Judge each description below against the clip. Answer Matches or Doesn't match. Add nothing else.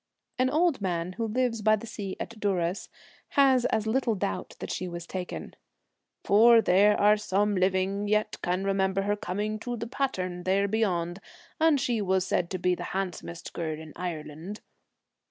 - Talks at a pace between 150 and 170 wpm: Doesn't match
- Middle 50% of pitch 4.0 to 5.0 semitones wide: Doesn't match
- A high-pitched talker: Matches